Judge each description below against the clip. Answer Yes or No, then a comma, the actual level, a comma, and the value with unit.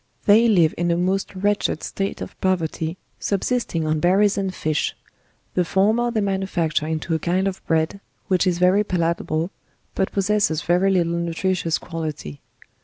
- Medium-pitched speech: Yes, medium, 180 Hz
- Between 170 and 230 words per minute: No, average, 155 wpm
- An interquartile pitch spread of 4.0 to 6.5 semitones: No, average, 3.1 semitones